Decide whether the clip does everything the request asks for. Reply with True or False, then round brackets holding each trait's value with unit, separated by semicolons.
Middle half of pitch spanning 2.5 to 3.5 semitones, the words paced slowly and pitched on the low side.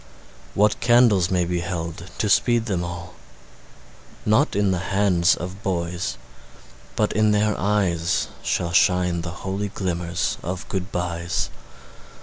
True (3.1 semitones; 130 wpm; 90 Hz)